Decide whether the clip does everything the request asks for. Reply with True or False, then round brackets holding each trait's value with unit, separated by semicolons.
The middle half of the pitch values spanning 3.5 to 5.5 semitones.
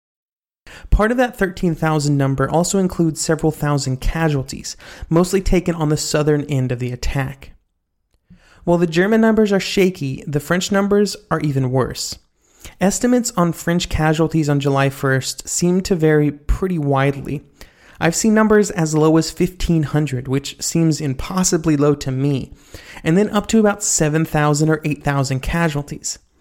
True (4.4 semitones)